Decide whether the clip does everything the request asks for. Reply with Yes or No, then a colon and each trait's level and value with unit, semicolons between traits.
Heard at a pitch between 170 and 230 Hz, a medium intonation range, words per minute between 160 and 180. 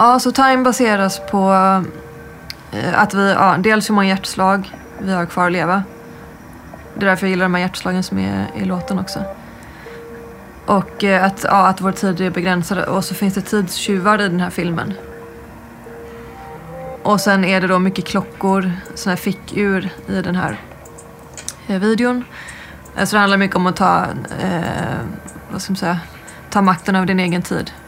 No: high, 190 Hz; narrow, 1.6 semitones; average, 170 wpm